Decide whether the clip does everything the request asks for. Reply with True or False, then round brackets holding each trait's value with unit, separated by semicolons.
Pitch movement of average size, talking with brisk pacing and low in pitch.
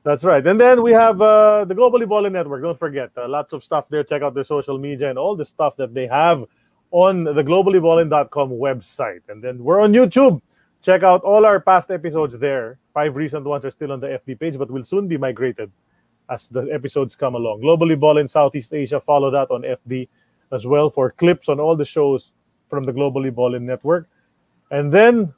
False (4.6 semitones; 210 wpm; 150 Hz)